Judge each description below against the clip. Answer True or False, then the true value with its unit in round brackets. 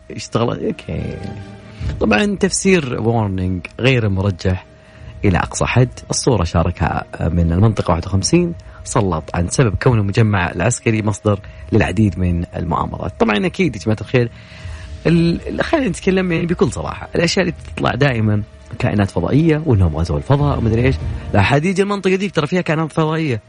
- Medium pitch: False (110 Hz)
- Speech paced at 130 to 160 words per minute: True (135 wpm)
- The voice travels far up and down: True (7.9 semitones)